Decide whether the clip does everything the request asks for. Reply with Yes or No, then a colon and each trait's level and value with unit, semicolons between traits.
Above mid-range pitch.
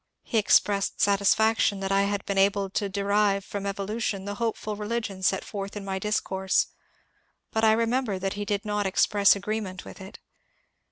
Yes: high, 200 Hz